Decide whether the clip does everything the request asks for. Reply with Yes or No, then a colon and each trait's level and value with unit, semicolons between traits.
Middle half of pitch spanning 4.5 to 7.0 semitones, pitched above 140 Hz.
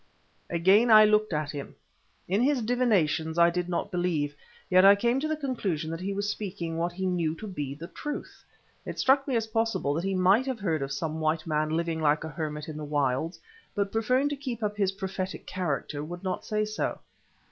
Yes: average, 5.2 semitones; medium, 185 Hz